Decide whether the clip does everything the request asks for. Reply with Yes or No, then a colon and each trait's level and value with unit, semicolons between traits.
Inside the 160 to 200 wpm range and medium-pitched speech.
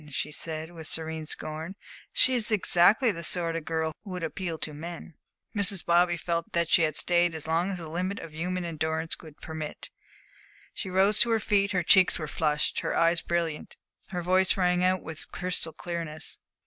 Yes: average, 190 wpm; medium, 170 Hz